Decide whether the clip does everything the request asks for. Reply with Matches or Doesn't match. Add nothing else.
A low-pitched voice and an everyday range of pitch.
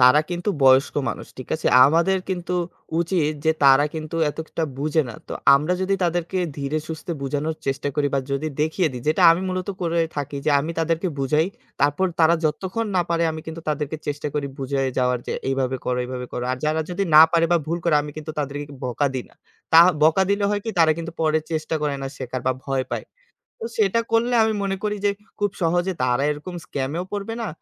Doesn't match